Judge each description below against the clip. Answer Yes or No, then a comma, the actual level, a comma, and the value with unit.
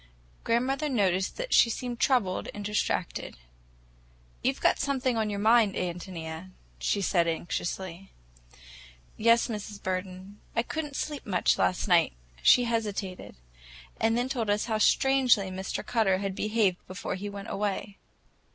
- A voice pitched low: No, high, 205 Hz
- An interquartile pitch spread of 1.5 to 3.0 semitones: No, average, 3.9 semitones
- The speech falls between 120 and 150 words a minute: Yes, average, 140 wpm